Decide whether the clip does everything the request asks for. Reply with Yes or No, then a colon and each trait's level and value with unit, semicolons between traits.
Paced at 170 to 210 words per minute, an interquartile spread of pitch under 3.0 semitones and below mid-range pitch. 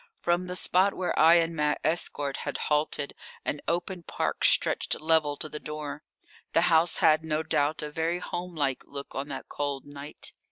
No: average, 175 wpm; narrow, 2.6 semitones; medium, 155 Hz